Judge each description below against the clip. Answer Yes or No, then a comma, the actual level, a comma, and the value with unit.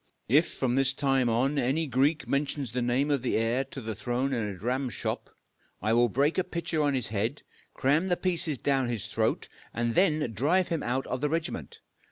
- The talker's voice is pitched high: No, low, 135 Hz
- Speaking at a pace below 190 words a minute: No, fast, 205 wpm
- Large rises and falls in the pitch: No, average, 3.7 semitones